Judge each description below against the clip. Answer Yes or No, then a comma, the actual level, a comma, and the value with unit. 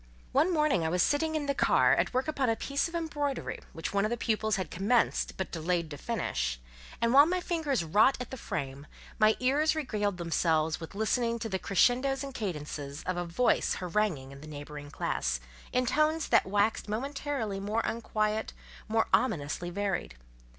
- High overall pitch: Yes, high, 215 Hz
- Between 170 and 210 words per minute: Yes, average, 185 wpm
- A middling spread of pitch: No, wide, 7.7 semitones